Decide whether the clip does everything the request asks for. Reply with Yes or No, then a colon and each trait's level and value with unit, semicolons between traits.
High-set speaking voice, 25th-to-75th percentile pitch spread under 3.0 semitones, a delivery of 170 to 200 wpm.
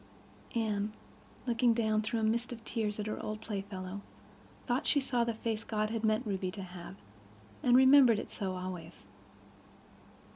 No: high, 215 Hz; narrow, 2.6 semitones; average, 160 wpm